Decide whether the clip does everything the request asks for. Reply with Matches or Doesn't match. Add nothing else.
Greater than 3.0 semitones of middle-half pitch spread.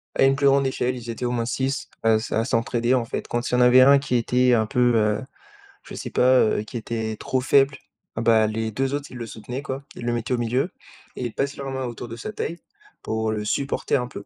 Doesn't match